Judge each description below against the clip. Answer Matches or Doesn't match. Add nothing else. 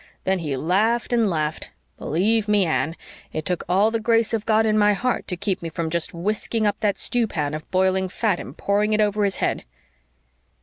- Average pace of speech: Doesn't match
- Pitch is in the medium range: Doesn't match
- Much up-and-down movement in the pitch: Doesn't match